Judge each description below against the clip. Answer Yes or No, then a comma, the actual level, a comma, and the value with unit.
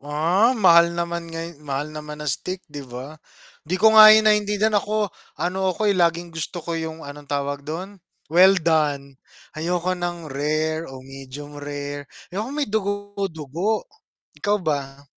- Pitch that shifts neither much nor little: Yes, average, 4.7 semitones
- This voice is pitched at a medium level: Yes, medium, 165 Hz